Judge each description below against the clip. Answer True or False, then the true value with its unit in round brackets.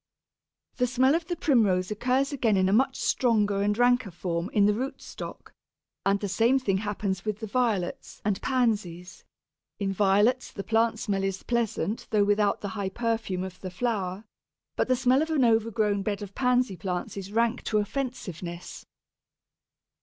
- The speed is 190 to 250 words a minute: False (170 wpm)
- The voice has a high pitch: True (210 Hz)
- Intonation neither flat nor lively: True (4.0 semitones)